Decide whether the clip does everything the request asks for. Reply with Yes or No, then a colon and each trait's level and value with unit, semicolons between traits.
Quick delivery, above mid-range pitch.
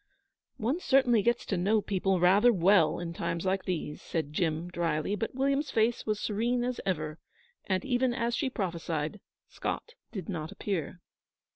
No: average, 160 wpm; high, 195 Hz